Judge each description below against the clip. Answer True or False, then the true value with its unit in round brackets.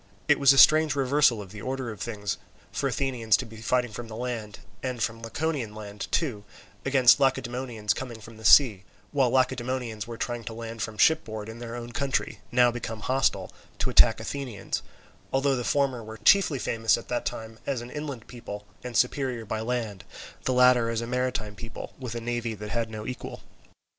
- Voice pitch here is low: True (120 Hz)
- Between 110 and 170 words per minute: False (195 wpm)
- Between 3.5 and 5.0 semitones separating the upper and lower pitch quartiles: False (2.7 semitones)